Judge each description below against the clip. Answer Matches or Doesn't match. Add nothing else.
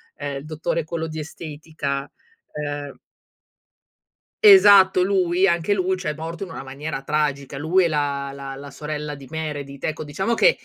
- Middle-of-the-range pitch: Matches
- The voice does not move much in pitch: Doesn't match